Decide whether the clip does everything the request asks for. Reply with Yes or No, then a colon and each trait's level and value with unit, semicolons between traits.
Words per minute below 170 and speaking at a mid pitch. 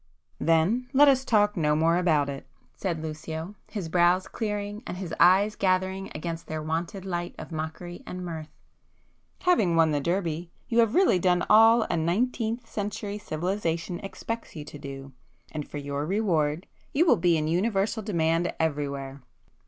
Yes: average, 160 wpm; medium, 175 Hz